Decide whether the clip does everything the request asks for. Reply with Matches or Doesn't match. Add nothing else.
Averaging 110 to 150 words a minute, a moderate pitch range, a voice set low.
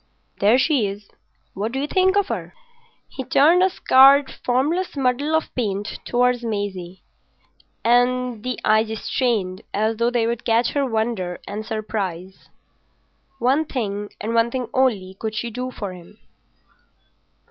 Doesn't match